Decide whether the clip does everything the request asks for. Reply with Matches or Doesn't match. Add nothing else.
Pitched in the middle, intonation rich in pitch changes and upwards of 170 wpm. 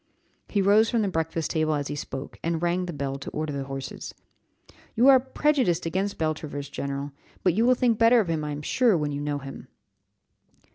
Matches